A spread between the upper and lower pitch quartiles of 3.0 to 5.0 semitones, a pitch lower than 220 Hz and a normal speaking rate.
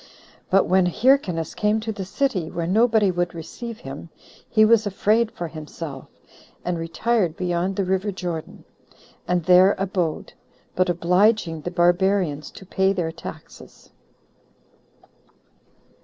No: average, 3.4 semitones; medium, 185 Hz; slow, 125 wpm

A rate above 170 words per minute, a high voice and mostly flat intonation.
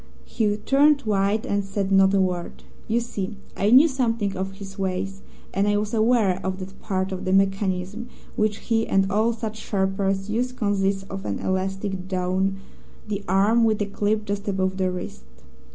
Yes: average, 180 wpm; high, 195 Hz; narrow, 2.0 semitones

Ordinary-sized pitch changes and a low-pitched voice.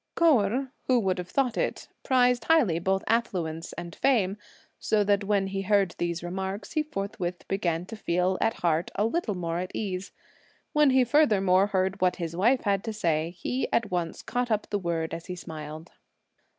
No: average, 4.4 semitones; high, 195 Hz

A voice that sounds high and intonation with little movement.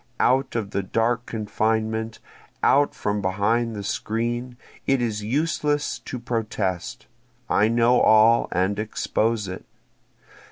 No: low, 115 Hz; narrow, 2.3 semitones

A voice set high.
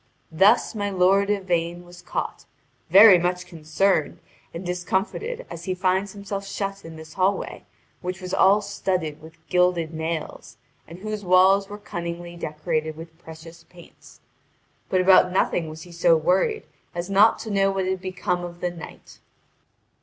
No: medium, 180 Hz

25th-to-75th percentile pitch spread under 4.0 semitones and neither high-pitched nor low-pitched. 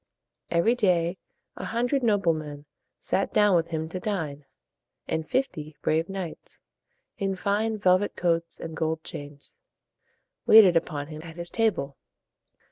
No: average, 4.4 semitones; medium, 170 Hz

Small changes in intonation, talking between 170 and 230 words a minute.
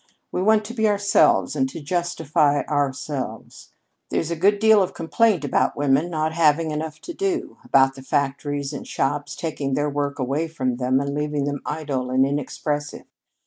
No: average, 3.2 semitones; average, 175 wpm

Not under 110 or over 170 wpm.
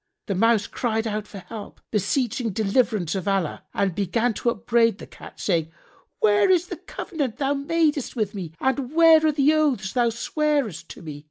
No: average, 185 wpm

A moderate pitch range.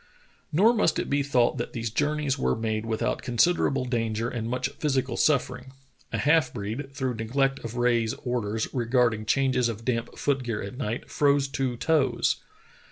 Yes: average, 3.1 semitones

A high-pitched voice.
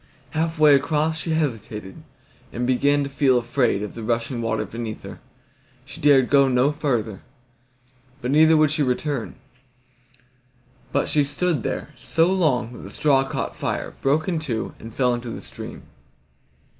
No: low, 135 Hz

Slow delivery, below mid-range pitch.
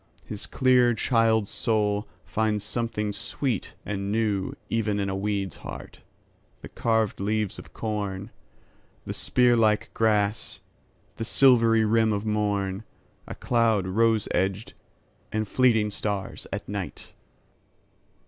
Yes: slow, 110 wpm; low, 105 Hz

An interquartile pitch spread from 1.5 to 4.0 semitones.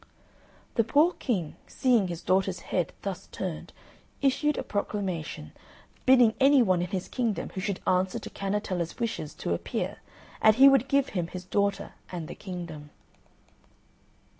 No: average, 5.1 semitones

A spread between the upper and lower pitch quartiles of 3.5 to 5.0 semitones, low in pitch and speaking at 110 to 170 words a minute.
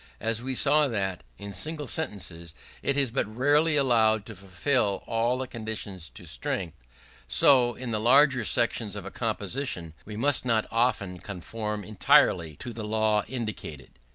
Yes: average, 4.2 semitones; low, 110 Hz; average, 155 wpm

